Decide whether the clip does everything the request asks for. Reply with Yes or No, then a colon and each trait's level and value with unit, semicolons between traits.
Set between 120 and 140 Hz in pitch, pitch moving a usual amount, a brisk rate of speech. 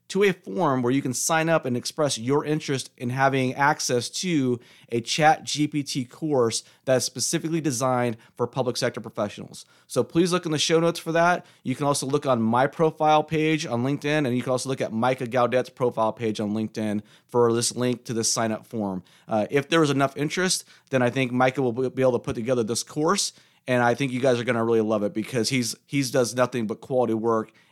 Yes: low, 130 Hz; average, 4.0 semitones; fast, 220 wpm